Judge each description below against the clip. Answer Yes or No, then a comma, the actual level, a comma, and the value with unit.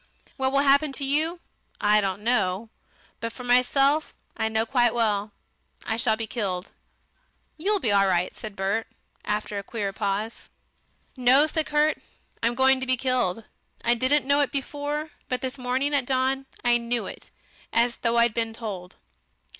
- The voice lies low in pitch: No, high, 240 Hz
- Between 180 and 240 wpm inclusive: No, average, 170 wpm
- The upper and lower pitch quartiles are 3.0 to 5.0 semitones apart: Yes, average, 3.9 semitones